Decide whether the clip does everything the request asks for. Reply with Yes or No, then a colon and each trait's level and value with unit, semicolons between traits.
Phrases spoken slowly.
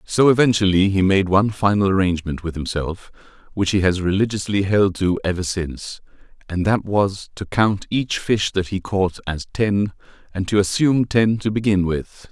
No: average, 175 wpm